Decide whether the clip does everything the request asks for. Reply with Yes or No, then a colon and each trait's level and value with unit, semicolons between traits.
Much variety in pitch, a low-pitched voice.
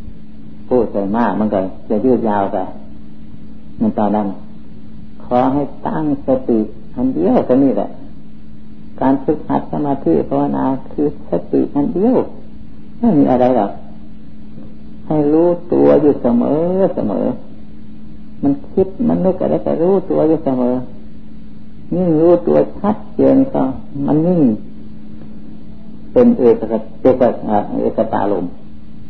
Yes: wide, 8.9 semitones; low, 130 Hz